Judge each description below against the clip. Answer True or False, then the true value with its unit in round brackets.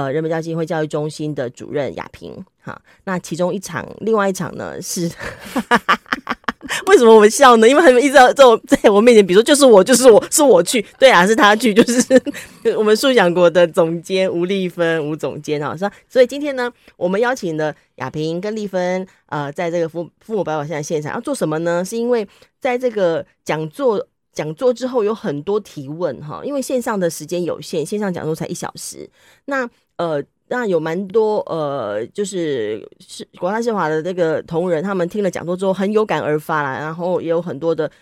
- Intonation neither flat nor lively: False (6.3 semitones)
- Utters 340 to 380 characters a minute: False (305 characters per minute)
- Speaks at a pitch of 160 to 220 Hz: True (190 Hz)